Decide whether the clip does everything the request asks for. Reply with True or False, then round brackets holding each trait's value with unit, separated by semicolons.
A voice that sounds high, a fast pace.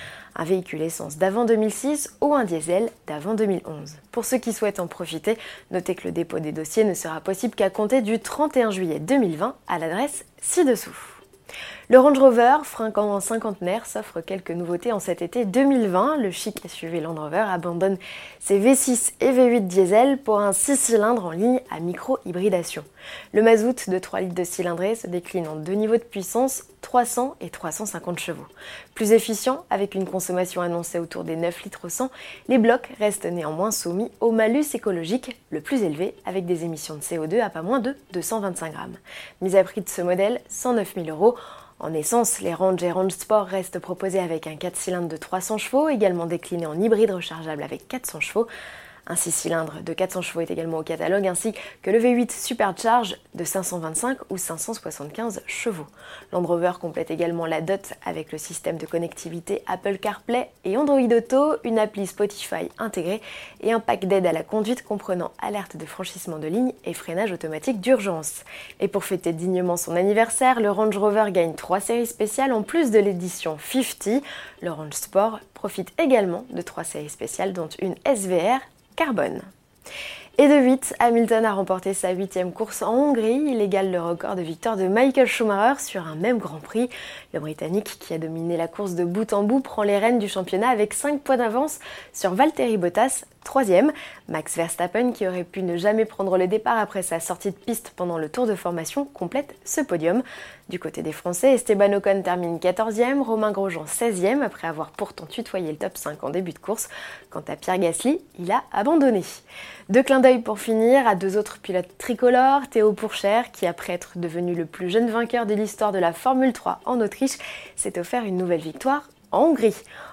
False (200 Hz; 185 wpm)